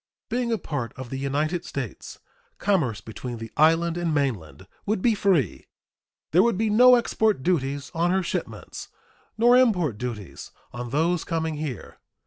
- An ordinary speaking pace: Yes, average, 155 wpm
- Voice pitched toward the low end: No, medium, 160 Hz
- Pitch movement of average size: No, wide, 7.1 semitones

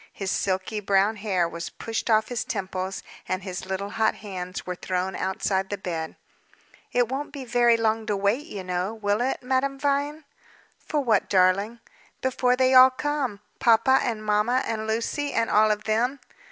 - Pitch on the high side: Yes, high, 220 Hz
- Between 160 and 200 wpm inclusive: Yes, average, 175 wpm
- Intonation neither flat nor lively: Yes, average, 4.6 semitones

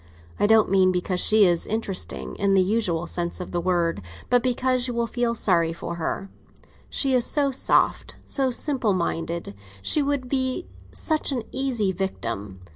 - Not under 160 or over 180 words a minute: Yes, average, 170 wpm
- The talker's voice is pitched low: No, high, 210 Hz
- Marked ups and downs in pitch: Yes, wide, 6.4 semitones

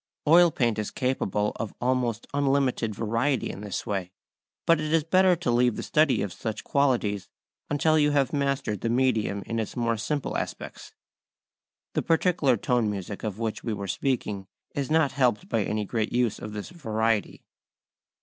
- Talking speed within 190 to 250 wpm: No, average, 170 wpm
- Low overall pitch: Yes, low, 120 Hz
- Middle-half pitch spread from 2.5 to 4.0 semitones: No, average, 4.9 semitones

